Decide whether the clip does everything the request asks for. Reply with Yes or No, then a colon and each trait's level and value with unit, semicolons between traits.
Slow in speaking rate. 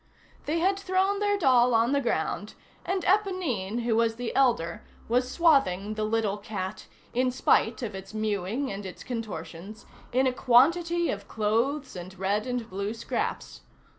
No: average, 160 wpm